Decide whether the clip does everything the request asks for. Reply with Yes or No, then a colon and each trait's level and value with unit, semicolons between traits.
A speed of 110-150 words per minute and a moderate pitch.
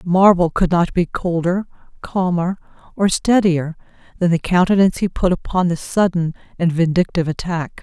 Yes: average, 145 wpm; medium, 175 Hz